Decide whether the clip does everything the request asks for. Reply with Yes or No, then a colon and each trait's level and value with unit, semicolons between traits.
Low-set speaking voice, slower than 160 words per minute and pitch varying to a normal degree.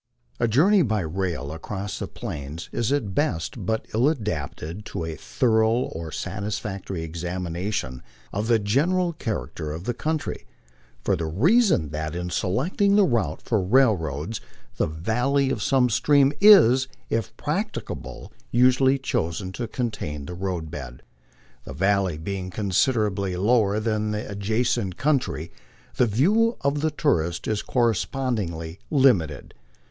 No: low, 105 Hz; average, 140 wpm; wide, 7.1 semitones